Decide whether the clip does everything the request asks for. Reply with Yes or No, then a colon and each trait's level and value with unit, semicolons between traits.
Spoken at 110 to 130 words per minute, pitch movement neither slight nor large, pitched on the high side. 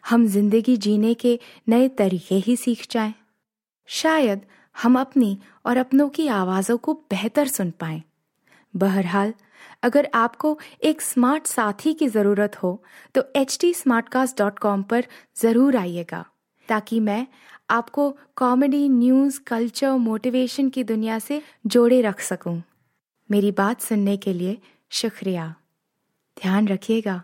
Yes: average, 120 wpm; average, 4.5 semitones; high, 230 Hz